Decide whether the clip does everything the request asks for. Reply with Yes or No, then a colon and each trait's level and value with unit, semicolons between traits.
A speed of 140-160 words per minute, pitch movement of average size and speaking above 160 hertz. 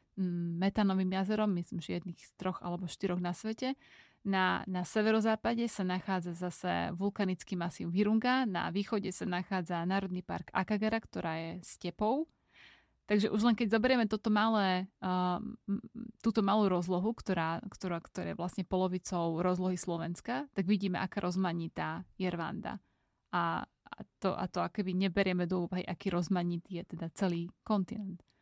Yes: average, 150 wpm; average, 3.0 semitones; high, 190 Hz